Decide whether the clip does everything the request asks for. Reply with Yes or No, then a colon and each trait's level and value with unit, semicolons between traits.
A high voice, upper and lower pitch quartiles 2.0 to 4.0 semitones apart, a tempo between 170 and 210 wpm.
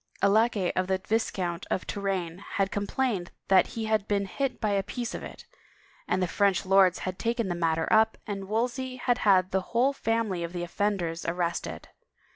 Yes: high, 195 Hz; average, 3.5 semitones; average, 190 wpm